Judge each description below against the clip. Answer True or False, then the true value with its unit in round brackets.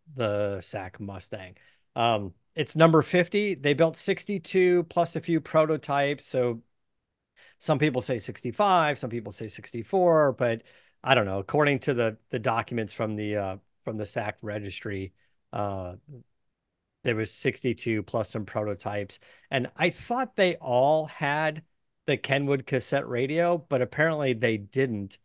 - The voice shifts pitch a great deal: True (6.5 semitones)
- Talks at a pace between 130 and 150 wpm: True (145 wpm)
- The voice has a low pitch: True (125 Hz)